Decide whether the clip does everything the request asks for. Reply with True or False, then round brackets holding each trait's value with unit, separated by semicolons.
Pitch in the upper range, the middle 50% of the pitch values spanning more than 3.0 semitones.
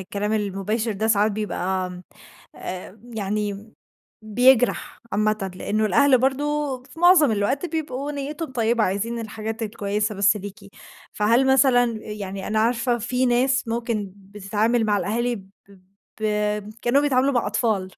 True (220 Hz; 3.4 semitones)